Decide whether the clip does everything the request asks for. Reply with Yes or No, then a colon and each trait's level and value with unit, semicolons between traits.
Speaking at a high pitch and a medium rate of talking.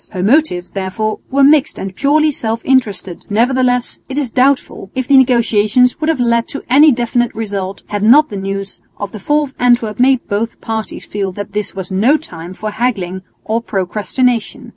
Yes: high, 230 Hz; average, 185 wpm